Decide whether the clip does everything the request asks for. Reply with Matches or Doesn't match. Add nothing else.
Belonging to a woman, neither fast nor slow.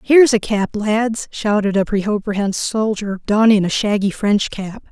Matches